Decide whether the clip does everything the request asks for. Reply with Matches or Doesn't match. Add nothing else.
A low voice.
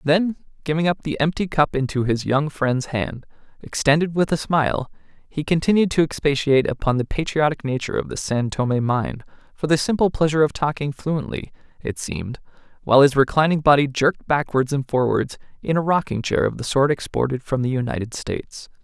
Doesn't match